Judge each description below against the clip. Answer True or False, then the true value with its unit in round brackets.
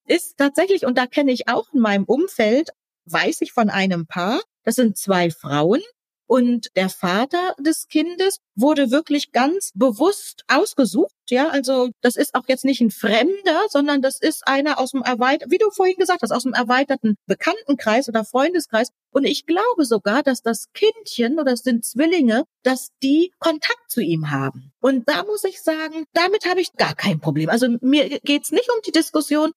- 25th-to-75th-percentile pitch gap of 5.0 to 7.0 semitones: True (5.6 semitones)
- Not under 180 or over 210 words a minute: True (185 wpm)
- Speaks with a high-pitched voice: True (270 Hz)